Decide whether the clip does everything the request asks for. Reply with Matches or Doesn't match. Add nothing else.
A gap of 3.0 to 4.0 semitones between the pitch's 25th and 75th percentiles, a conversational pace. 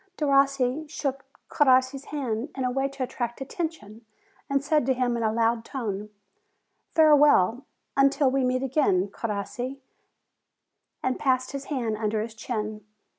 Matches